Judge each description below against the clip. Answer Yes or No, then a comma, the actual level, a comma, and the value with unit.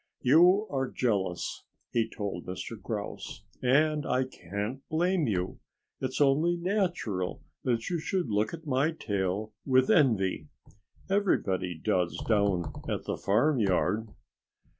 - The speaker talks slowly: Yes, slow, 120 wpm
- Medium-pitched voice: No, low, 120 Hz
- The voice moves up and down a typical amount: No, wide, 7.5 semitones